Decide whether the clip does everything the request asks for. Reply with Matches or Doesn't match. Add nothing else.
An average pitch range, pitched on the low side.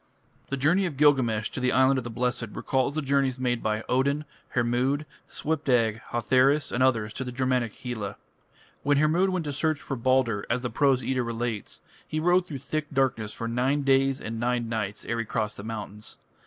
Matches